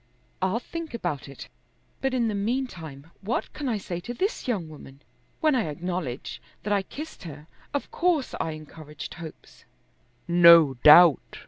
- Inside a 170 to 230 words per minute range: No, average, 155 wpm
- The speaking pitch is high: No, medium, 180 Hz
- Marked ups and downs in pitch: Yes, wide, 7.8 semitones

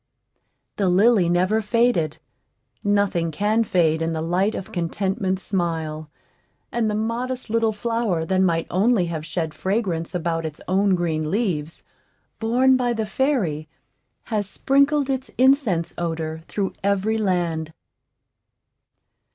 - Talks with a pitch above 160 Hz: Yes, high, 190 Hz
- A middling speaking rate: No, slow, 125 wpm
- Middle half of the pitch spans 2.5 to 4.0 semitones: No, average, 5.1 semitones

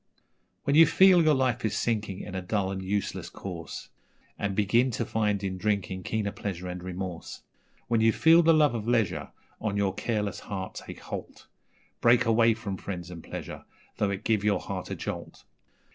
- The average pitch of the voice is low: Yes, low, 105 Hz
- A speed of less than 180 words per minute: No, average, 185 wpm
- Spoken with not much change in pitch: No, average, 3.5 semitones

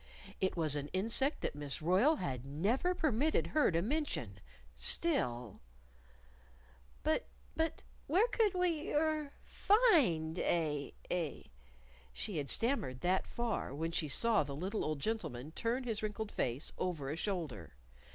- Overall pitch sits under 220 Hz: Yes, medium, 185 Hz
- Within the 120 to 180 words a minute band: Yes, average, 140 wpm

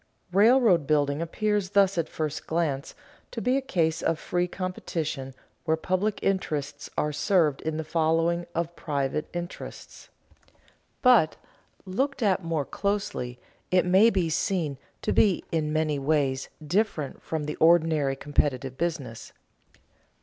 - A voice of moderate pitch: Yes, medium, 165 Hz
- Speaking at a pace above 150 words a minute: No, slow, 135 wpm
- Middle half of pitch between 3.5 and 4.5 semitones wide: Yes, average, 3.8 semitones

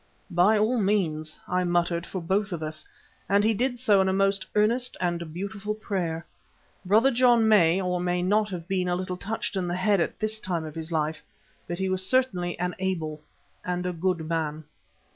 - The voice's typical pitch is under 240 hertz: Yes, medium, 185 Hz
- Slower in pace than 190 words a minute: No, average, 200 wpm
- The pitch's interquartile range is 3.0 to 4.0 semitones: Yes, average, 3.3 semitones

